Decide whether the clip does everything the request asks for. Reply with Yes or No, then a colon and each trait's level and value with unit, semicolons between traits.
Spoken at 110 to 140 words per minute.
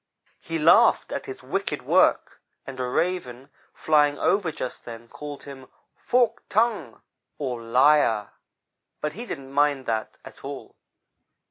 Yes: slow, 135 wpm